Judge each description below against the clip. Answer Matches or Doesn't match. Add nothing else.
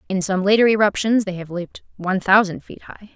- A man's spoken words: Doesn't match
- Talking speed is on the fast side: Matches